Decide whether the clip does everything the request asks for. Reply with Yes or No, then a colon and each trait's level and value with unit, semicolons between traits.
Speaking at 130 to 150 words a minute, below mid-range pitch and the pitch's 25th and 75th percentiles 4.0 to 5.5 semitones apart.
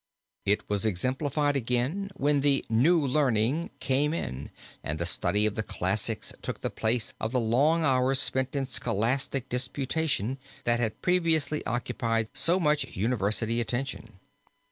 Yes: average, 145 wpm; low, 130 Hz; average, 4.4 semitones